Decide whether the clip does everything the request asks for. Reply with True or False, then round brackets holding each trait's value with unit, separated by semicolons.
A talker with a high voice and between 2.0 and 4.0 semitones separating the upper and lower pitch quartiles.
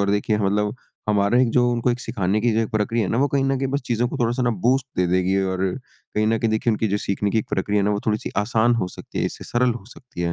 False (110 Hz; 3.0 semitones)